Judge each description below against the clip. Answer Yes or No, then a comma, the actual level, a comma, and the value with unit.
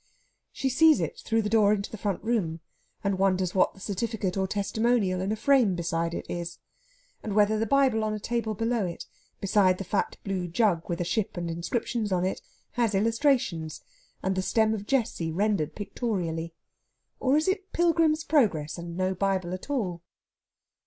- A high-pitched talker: Yes, high, 200 Hz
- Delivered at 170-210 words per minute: Yes, average, 180 wpm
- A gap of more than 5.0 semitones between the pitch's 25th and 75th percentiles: No, average, 4.1 semitones